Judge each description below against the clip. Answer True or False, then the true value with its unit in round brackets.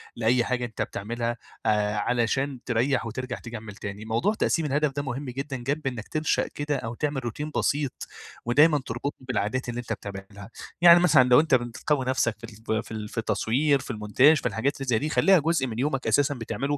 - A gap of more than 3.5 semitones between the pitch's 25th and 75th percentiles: True (4.1 semitones)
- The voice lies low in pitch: True (125 Hz)